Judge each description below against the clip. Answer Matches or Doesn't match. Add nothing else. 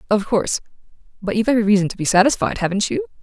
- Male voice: Doesn't match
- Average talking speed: Matches